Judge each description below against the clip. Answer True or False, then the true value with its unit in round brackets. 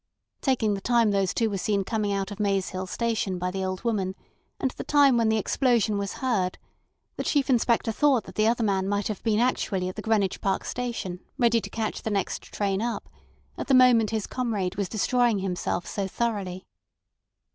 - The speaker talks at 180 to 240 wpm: True (200 wpm)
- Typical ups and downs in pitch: True (3.3 semitones)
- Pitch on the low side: False (215 Hz)